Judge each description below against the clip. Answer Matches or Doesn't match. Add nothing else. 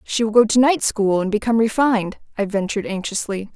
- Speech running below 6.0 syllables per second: Doesn't match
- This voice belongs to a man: Doesn't match